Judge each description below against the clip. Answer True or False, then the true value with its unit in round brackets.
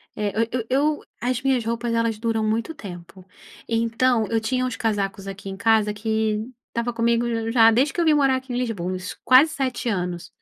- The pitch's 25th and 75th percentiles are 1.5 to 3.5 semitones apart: True (3.1 semitones)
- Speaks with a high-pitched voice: True (230 Hz)